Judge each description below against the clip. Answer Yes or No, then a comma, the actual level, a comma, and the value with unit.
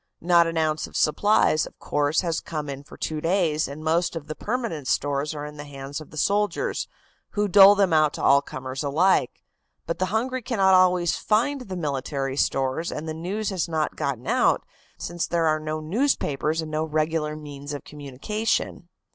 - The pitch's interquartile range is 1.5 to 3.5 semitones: No, average, 4.1 semitones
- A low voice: No, medium, 155 Hz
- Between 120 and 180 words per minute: No, average, 190 wpm